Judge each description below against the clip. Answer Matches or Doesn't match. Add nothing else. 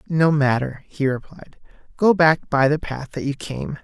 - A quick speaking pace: Doesn't match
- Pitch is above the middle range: Doesn't match